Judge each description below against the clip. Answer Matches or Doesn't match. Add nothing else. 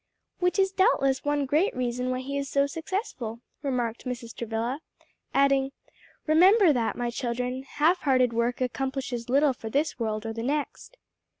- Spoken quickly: Doesn't match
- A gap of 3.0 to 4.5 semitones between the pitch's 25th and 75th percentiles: Matches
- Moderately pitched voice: Doesn't match